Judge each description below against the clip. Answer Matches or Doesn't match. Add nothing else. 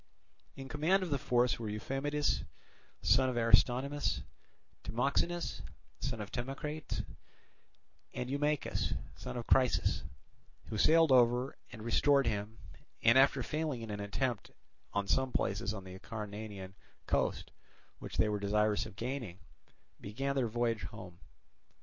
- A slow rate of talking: Matches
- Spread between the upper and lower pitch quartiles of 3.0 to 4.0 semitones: Doesn't match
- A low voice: Matches